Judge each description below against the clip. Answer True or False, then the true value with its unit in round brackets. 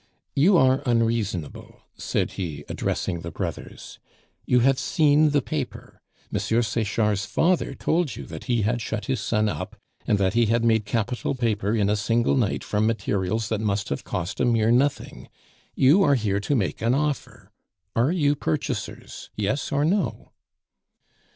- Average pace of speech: True (165 wpm)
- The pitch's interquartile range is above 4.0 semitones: True (4.6 semitones)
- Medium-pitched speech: False (115 Hz)